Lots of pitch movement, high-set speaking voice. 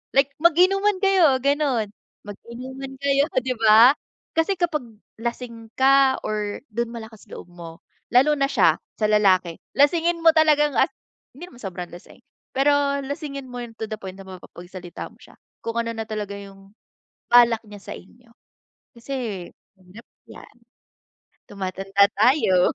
Yes: wide, 5.7 semitones; high, 235 Hz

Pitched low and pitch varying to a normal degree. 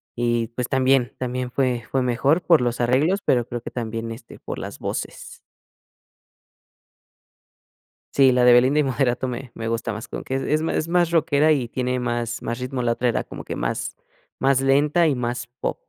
No: low, 125 Hz; narrow, 2.2 semitones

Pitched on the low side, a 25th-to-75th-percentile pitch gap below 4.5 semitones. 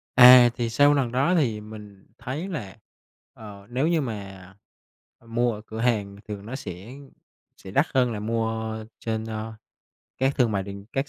Yes: low, 115 Hz; average, 3.4 semitones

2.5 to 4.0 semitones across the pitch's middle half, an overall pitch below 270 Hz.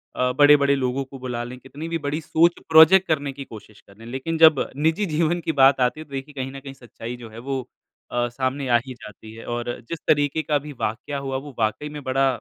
Yes: average, 3.2 semitones; low, 135 Hz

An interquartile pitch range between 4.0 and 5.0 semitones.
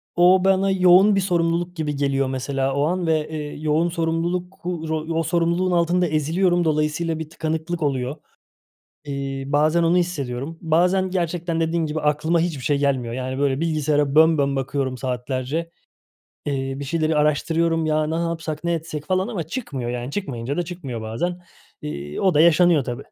No: average, 3.5 semitones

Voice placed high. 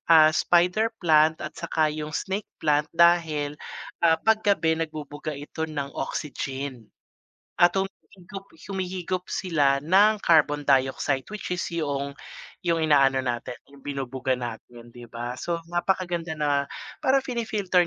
No: medium, 155 Hz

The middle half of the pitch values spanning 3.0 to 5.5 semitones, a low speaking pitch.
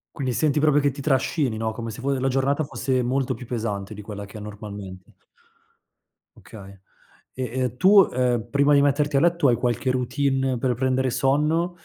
Yes: average, 3.7 semitones; low, 130 Hz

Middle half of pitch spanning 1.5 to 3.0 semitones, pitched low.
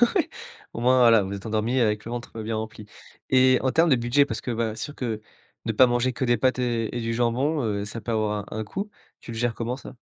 Yes: average, 2.7 semitones; low, 120 Hz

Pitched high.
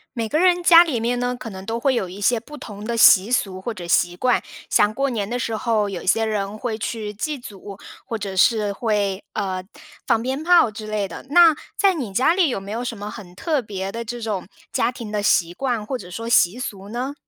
Yes: high, 225 Hz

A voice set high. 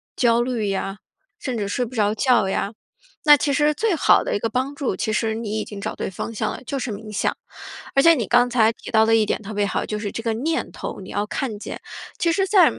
Yes: high, 230 Hz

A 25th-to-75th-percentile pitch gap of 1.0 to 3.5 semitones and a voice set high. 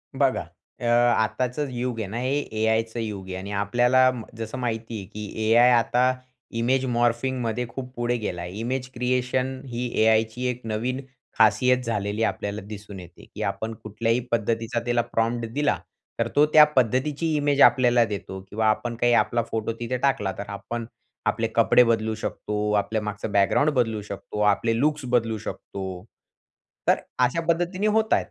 No: average, 2.9 semitones; low, 115 Hz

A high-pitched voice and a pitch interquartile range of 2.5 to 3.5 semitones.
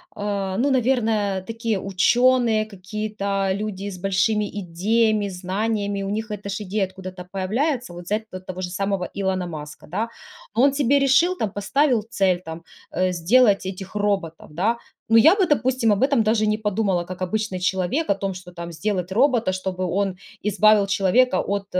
Yes: high, 200 Hz; average, 3.2 semitones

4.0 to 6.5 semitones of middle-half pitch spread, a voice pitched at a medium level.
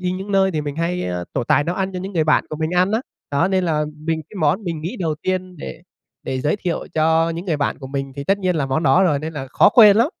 No: average, 3.6 semitones; medium, 165 Hz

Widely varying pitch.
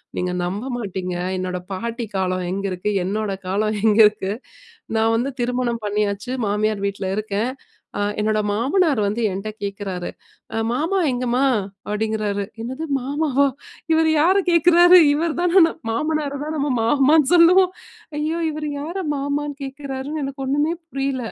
Yes: wide, 6.2 semitones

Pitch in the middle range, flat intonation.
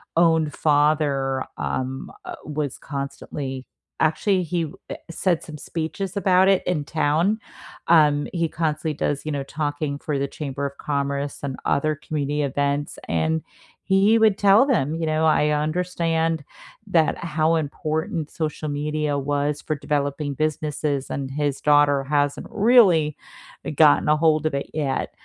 Yes: medium, 150 Hz; narrow, 2.2 semitones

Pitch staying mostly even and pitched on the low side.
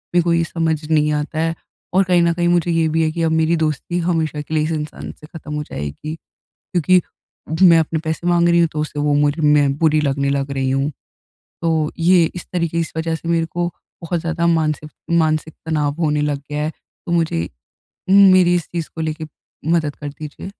No: narrow, 2.1 semitones; medium, 160 Hz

